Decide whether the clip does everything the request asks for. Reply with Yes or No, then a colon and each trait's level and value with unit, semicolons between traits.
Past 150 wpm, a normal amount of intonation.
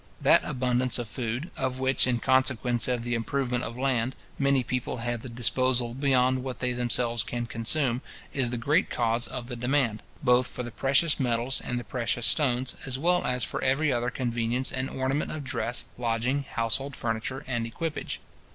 No: average, 180 wpm; narrow, 1.9 semitones